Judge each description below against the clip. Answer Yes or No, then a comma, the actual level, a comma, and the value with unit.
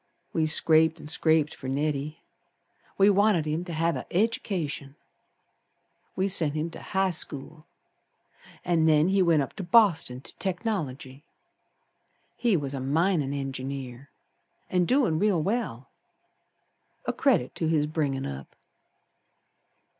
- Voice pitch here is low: No, medium, 160 Hz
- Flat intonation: No, average, 4.5 semitones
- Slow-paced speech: Yes, slow, 130 wpm